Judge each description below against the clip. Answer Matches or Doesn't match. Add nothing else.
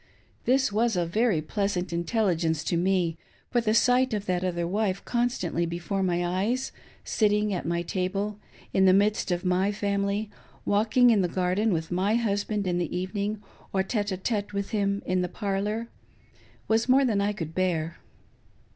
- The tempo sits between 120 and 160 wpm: Doesn't match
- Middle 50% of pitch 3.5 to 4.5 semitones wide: Doesn't match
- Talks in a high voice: Matches